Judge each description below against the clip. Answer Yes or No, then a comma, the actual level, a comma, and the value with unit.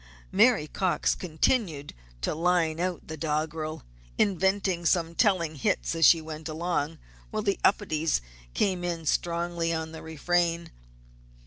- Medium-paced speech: No, slow, 130 wpm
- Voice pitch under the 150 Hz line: No, medium, 165 Hz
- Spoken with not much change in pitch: Yes, narrow, 2.2 semitones